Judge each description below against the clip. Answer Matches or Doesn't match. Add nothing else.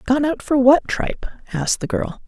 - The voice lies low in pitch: Doesn't match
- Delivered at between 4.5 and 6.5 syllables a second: Matches